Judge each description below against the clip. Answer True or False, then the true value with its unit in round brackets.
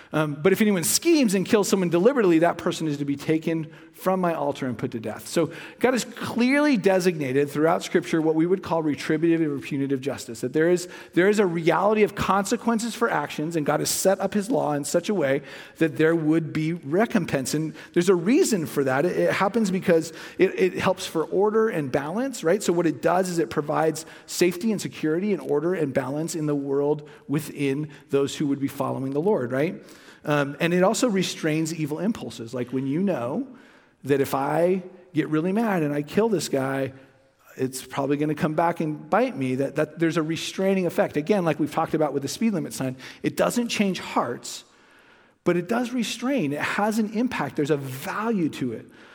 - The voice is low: False (165 Hz)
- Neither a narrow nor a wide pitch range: True (4.8 semitones)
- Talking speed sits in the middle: False (210 wpm)